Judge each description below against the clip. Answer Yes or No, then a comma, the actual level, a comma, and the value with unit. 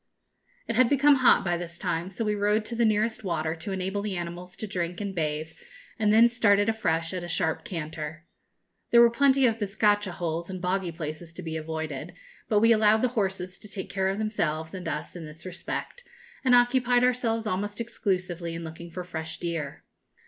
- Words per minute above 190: Yes, average, 200 wpm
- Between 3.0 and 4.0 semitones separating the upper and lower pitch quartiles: No, average, 4.6 semitones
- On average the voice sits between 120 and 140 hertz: No, high, 190 Hz